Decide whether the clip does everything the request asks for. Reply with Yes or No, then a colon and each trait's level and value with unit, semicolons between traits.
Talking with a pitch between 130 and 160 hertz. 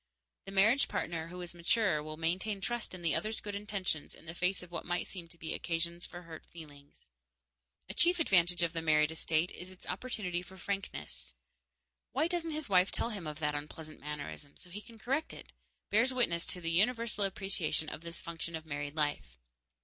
No: medium, 175 Hz